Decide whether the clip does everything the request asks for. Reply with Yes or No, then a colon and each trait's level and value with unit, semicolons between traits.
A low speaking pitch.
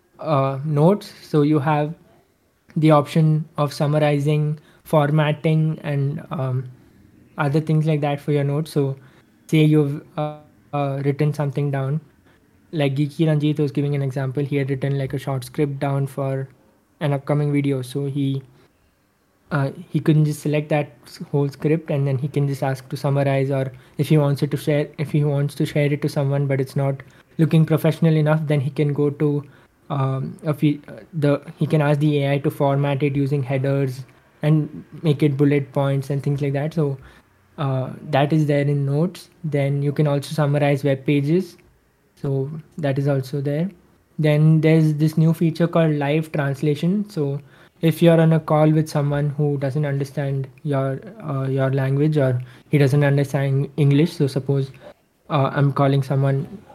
No: medium, 145 Hz